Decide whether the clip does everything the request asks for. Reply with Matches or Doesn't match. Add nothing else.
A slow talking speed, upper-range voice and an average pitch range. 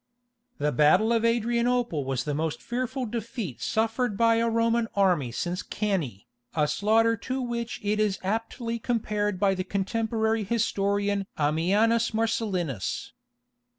Matches